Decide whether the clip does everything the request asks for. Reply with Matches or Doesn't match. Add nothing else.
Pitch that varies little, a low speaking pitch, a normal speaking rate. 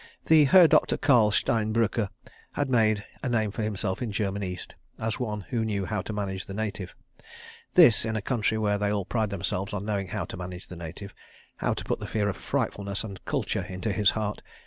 Doesn't match